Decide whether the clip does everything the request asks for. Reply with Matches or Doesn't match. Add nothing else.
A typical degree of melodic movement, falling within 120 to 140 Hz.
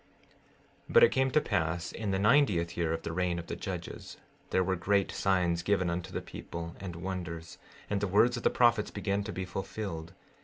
Doesn't match